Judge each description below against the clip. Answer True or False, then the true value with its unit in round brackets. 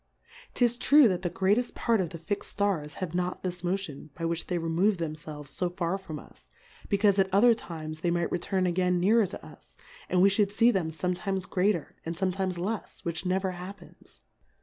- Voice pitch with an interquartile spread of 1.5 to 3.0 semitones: True (2.7 semitones)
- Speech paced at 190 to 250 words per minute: True (200 wpm)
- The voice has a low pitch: False (185 Hz)